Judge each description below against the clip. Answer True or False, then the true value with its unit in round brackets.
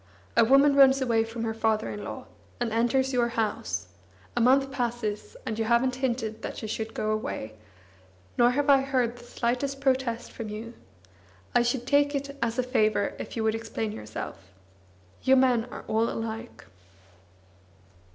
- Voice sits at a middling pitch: False (235 Hz)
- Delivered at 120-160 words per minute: False (170 wpm)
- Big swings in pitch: False (2.8 semitones)